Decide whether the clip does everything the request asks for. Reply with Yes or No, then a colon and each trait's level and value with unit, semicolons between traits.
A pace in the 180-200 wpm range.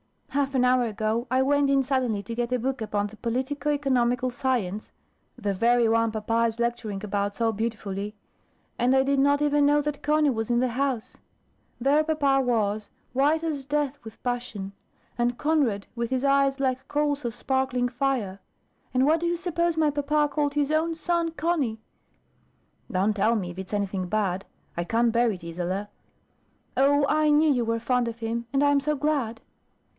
Yes: average, 185 wpm